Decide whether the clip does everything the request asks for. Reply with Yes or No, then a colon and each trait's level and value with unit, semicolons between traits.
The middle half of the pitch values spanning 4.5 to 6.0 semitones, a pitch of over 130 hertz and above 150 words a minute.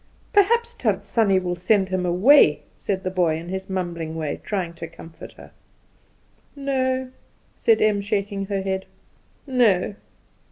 No: average, 5.2 semitones; high, 190 Hz; average, 145 wpm